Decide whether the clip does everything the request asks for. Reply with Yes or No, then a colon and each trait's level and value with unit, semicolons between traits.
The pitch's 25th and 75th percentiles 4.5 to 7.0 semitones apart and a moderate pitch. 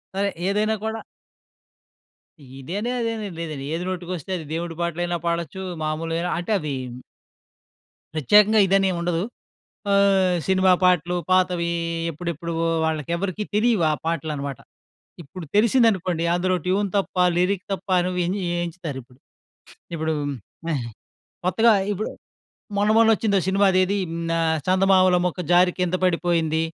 No: average, 2.9 semitones; medium, 180 Hz